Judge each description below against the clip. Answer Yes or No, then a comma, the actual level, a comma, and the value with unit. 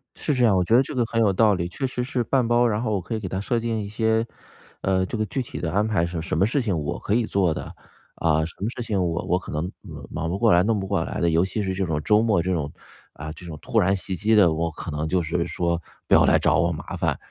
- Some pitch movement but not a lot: Yes, average, 4.7 semitones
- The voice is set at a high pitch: No, very low, 95 Hz